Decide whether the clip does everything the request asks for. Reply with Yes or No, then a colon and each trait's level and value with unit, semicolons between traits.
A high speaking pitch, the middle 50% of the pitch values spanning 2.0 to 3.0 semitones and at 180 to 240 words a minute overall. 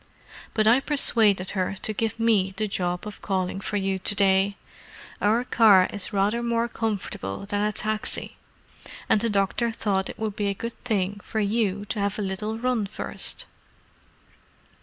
No: high, 205 Hz; narrow, 2.4 semitones; average, 170 wpm